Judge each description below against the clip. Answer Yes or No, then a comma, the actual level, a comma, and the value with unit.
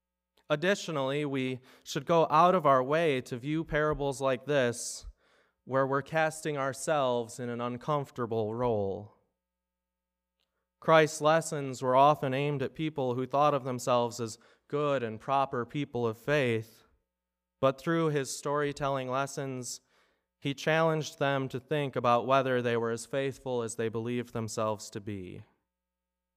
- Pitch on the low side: Yes, low, 130 Hz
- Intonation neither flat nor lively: Yes, average, 4.2 semitones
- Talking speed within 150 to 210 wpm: No, average, 140 wpm